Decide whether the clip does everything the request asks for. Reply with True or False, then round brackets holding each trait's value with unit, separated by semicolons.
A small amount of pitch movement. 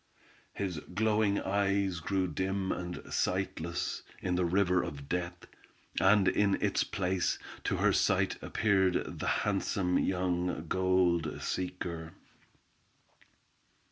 True (1.8 semitones)